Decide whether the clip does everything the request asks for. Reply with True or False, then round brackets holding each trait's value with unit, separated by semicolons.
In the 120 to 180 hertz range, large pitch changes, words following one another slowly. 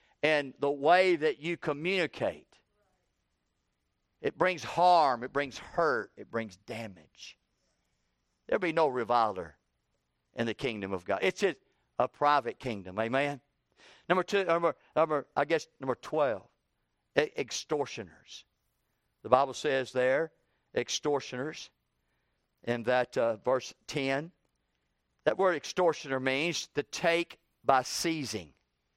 True (135 Hz; 6.5 semitones; 115 wpm)